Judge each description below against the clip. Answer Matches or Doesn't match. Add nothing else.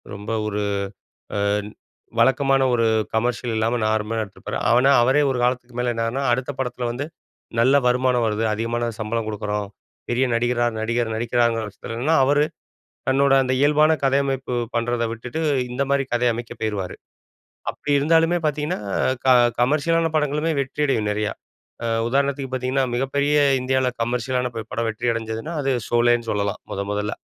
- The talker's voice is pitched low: Matches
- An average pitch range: Matches